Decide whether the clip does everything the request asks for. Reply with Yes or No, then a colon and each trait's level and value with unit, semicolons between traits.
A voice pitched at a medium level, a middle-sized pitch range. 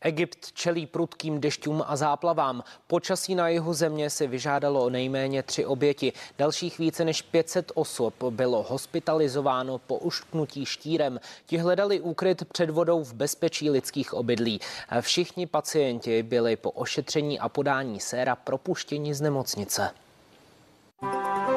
Yes: medium, 150 Hz; average, 4.2 semitones